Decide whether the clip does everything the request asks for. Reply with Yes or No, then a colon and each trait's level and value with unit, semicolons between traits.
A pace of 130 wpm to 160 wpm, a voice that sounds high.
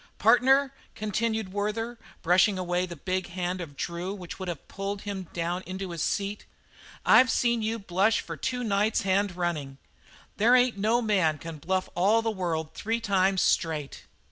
No: average, 170 wpm; high, 195 Hz